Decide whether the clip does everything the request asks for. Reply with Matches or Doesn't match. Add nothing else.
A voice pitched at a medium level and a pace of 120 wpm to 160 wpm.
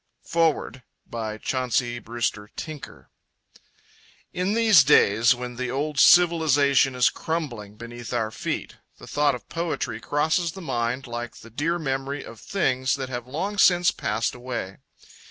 Doesn't match